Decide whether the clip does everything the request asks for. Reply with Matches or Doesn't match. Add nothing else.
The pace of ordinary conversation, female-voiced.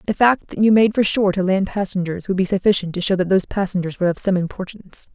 Doesn't match